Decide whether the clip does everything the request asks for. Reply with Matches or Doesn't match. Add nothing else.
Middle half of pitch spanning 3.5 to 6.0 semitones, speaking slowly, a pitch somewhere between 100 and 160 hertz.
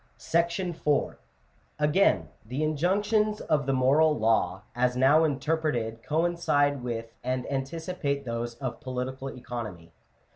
Matches